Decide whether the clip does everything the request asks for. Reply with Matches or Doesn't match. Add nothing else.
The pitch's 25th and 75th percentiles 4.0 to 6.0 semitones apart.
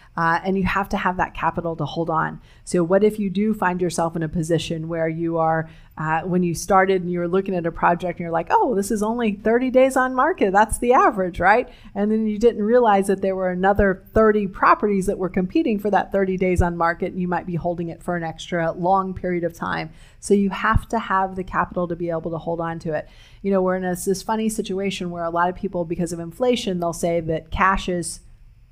Doesn't match